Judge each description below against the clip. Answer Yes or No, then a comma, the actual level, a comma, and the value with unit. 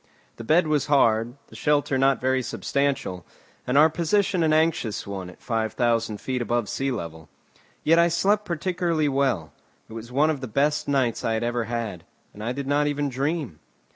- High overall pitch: No, low, 135 Hz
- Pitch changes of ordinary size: Yes, average, 4.9 semitones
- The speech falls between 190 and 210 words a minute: Yes, average, 195 wpm